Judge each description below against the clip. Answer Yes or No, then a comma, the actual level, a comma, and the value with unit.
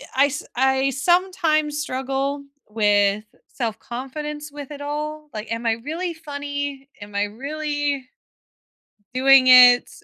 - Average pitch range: Yes, average, 3.2 semitones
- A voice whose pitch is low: No, very high, 275 Hz